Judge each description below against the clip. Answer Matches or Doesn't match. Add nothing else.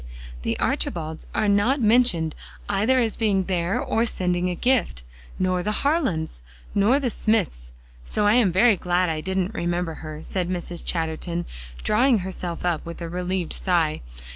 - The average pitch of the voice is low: Doesn't match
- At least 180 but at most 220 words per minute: Doesn't match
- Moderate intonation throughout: Matches